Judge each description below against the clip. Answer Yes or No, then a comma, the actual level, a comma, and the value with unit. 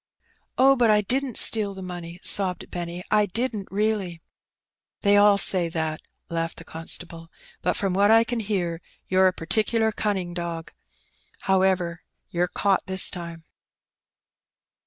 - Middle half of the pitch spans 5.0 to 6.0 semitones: No, average, 3.5 semitones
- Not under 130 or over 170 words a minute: Yes, average, 140 wpm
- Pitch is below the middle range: No, high, 190 Hz